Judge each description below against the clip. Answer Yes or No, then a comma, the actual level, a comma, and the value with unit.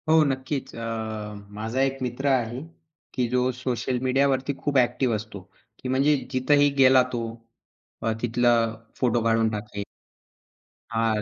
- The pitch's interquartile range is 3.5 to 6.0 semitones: No, narrow, 2.6 semitones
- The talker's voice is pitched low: Yes, low, 125 Hz